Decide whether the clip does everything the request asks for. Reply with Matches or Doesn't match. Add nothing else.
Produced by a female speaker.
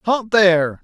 Doesn't match